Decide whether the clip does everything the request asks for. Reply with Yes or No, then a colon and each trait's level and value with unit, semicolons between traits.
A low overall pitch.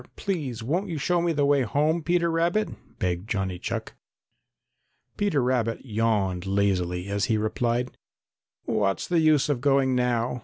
Yes: low, 125 Hz